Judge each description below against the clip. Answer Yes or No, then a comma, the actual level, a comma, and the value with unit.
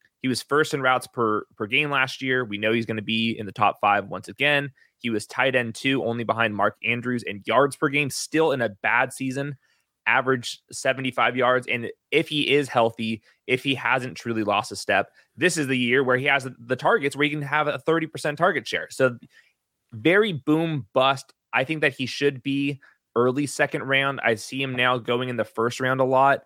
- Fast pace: Yes, fast, 220 wpm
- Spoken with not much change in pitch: No, average, 3.4 semitones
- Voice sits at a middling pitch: No, low, 130 Hz